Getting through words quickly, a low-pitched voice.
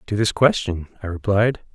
No: average, 170 wpm; low, 100 Hz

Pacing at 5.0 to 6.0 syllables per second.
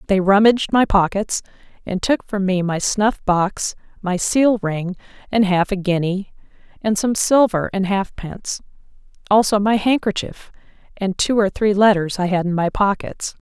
No: 4.6 syllables/s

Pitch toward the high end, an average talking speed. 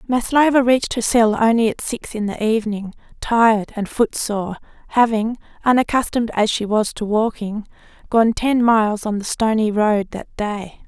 Yes: high, 220 Hz; average, 160 wpm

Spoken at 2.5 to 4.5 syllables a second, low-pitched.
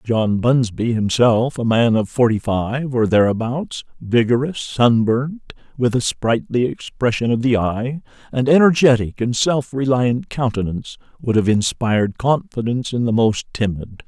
Yes: 4.4 syllables/s; low, 120 Hz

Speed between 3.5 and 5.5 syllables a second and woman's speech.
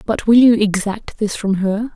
Yes: 4.4 syllables/s; female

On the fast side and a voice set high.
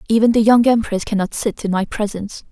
Yes: fast, 215 wpm; high, 215 Hz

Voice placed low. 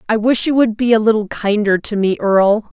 No: high, 215 Hz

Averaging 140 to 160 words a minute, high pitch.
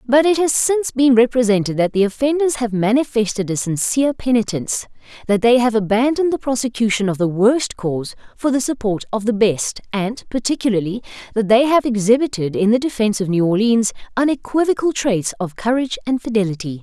No: average, 170 wpm; high, 230 Hz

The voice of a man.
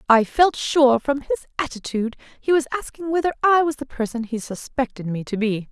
No: female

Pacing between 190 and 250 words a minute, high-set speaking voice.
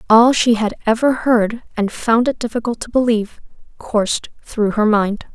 No: average, 170 wpm; high, 225 Hz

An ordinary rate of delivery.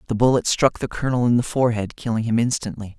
No: fast, 220 wpm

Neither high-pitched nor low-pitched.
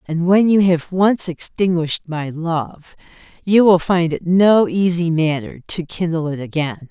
Yes: medium, 170 Hz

